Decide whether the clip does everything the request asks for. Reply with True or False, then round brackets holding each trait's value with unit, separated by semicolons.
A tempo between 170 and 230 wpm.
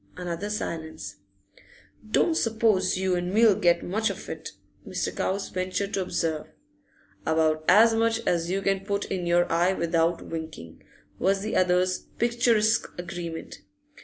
False (145 wpm)